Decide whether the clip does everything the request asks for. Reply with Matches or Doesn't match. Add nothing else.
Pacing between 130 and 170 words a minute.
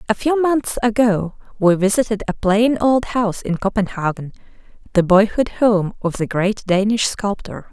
Matches